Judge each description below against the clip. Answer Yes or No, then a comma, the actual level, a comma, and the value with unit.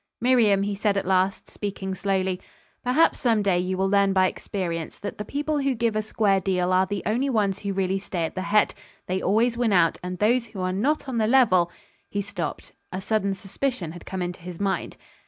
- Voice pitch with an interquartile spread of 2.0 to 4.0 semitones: Yes, average, 2.9 semitones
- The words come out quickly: Yes, fast, 220 wpm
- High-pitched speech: Yes, high, 200 Hz